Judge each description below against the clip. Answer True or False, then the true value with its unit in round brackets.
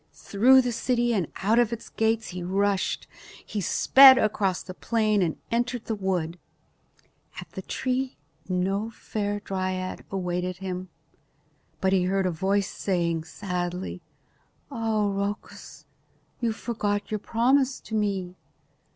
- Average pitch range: True (3.5 semitones)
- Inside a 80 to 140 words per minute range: True (135 wpm)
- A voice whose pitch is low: False (200 Hz)